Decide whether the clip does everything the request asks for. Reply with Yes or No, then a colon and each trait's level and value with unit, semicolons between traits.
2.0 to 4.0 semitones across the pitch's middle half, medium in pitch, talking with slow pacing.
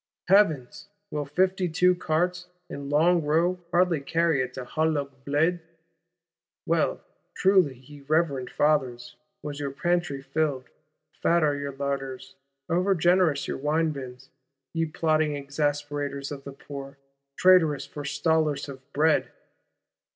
Yes: average, 3.2 semitones; medium, 150 Hz; slow, 130 wpm